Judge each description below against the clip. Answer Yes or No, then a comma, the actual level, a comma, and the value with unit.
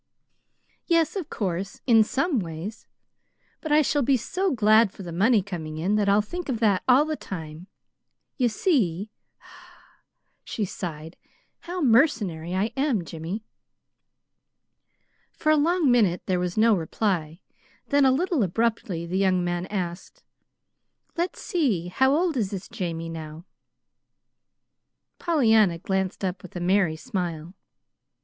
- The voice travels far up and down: Yes, wide, 7.0 semitones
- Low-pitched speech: No, high, 205 Hz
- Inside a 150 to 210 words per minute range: No, average, 140 wpm